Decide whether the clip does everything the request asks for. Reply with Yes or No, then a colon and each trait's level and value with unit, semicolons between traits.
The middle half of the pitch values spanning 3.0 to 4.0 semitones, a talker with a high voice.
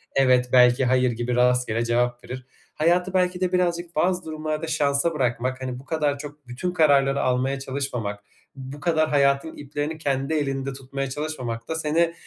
No: average, 3.7 semitones; medium, 140 Hz